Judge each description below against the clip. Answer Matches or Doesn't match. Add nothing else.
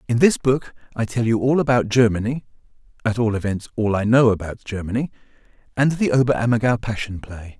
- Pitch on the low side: Matches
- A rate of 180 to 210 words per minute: Doesn't match